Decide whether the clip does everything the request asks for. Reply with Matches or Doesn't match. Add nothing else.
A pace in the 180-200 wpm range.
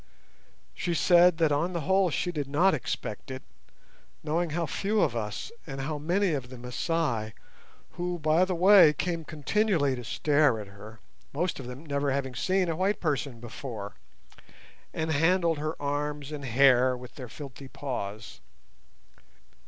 Doesn't match